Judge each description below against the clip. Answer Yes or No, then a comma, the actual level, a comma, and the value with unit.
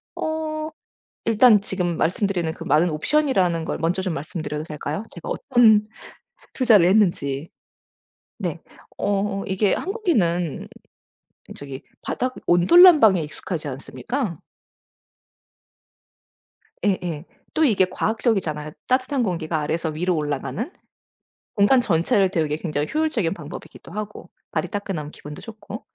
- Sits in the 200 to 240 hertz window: No, medium, 185 Hz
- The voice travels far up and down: Yes, wide, 5.9 semitones